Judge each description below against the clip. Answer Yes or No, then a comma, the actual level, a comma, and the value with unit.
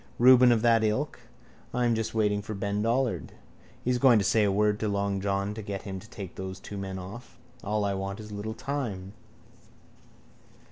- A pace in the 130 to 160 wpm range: No, average, 195 wpm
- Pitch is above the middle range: No, low, 105 Hz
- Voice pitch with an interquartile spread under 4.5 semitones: Yes, average, 2.8 semitones